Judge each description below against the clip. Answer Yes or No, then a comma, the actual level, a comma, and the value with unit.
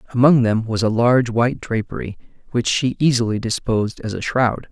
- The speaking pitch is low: Yes, low, 115 Hz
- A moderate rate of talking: Yes, average, 180 wpm